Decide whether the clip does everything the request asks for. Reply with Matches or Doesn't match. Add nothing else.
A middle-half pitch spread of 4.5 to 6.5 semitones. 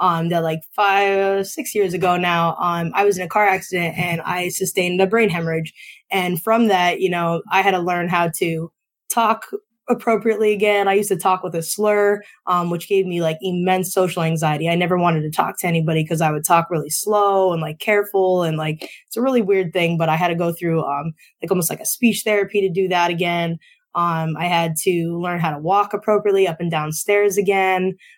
Doesn't match